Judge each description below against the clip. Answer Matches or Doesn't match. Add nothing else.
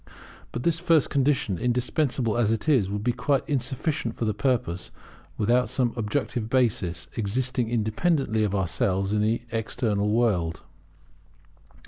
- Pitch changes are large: Doesn't match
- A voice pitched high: Doesn't match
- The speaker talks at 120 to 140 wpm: Matches